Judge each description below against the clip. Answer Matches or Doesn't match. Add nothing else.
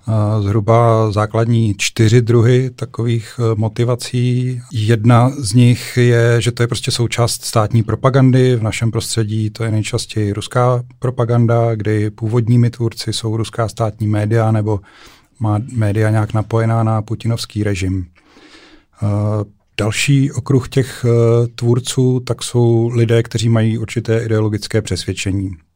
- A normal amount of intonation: Doesn't match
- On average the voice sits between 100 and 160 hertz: Matches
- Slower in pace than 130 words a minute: Matches